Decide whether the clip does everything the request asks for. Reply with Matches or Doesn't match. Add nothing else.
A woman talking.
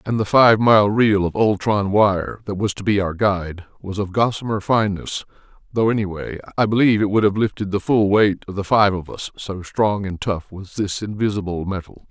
Doesn't match